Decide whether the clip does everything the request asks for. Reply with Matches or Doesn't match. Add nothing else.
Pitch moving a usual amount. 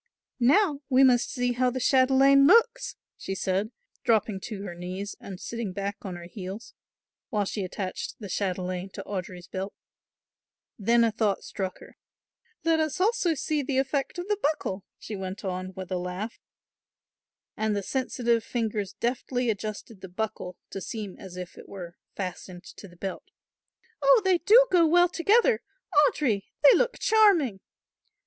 Doesn't match